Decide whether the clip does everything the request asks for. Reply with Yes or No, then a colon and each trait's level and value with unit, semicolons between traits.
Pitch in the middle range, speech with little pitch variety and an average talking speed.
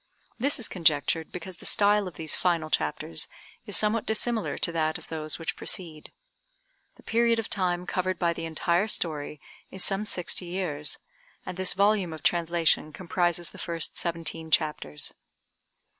No: medium, 175 Hz; average, 3.3 semitones; average, 160 wpm